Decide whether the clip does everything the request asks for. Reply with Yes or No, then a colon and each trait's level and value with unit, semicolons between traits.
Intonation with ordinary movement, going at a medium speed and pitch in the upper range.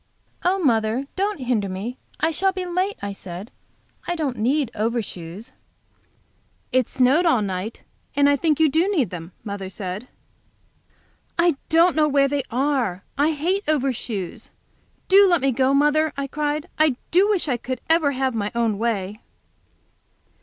No: wide, 6.3 semitones; average, 160 wpm; very high, 275 Hz